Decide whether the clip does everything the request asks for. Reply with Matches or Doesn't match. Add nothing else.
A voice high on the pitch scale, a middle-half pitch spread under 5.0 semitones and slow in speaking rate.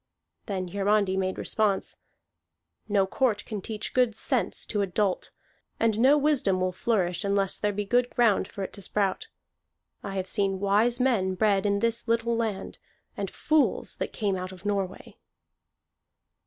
Doesn't match